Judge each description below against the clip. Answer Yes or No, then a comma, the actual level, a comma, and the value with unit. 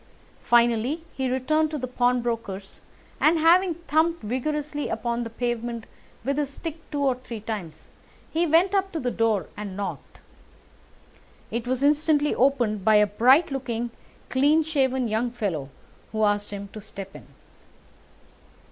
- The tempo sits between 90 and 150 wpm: Yes, average, 145 wpm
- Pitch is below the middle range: No, very high, 250 Hz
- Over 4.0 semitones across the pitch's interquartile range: Yes, average, 5.2 semitones